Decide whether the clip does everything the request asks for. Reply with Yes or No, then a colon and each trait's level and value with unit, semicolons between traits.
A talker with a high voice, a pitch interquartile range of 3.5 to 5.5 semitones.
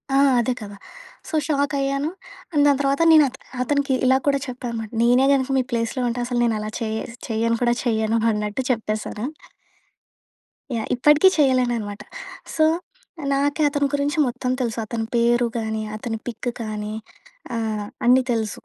Yes: high, 240 Hz; average, 3.8 semitones